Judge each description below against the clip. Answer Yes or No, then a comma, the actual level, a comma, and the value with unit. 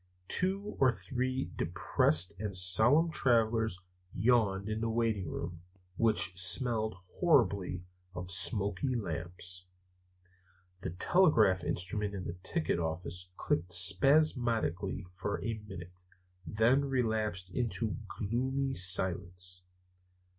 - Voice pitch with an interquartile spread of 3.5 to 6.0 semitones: Yes, average, 4.8 semitones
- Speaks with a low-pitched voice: Yes, low, 100 Hz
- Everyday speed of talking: No, slow, 110 wpm